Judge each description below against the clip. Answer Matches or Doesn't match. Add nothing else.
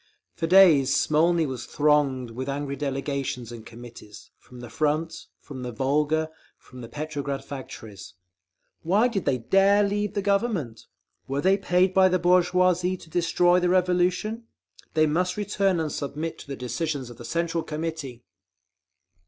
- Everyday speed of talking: Matches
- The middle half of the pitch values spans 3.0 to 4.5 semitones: Doesn't match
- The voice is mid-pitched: Matches